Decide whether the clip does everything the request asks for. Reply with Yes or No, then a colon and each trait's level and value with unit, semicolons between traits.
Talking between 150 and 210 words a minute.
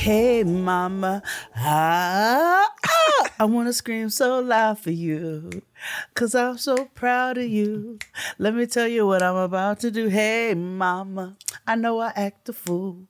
Yes: average, 155 wpm